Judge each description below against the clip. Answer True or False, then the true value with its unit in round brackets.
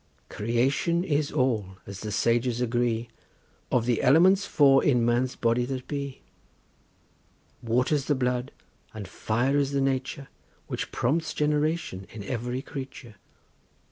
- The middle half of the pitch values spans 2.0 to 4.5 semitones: True (3.2 semitones)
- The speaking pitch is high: False (125 Hz)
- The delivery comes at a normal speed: False (130 wpm)